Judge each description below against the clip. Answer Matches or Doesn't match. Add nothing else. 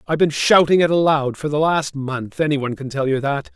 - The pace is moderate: Doesn't match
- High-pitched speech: Doesn't match